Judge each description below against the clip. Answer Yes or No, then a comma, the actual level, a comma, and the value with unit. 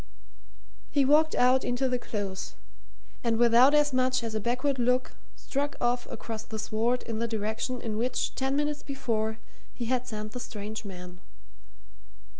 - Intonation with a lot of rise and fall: No, average, 2.9 semitones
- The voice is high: Yes, high, 240 Hz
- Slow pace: No, average, 160 wpm